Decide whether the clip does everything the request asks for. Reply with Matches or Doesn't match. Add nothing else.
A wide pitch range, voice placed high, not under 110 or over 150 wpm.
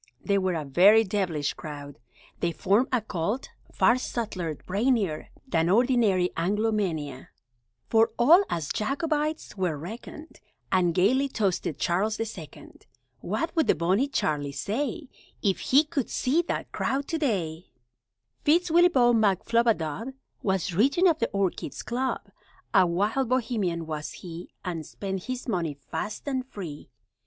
Matches